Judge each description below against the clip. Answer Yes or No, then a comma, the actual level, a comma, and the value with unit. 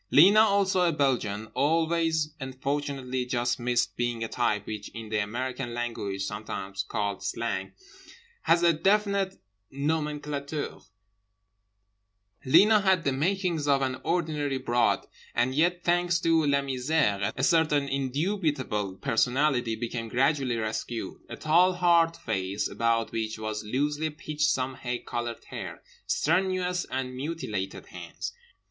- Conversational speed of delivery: No, slow, 130 wpm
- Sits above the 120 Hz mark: Yes, low, 135 Hz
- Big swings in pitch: Yes, wide, 5.7 semitones